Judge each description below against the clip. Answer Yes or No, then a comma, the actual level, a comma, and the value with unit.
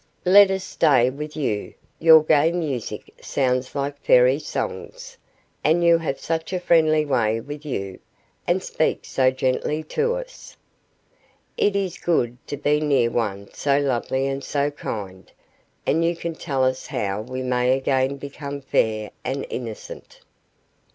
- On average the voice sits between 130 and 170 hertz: Yes, medium, 140 Hz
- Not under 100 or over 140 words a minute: No, average, 150 wpm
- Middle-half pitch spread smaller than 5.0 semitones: Yes, average, 3.9 semitones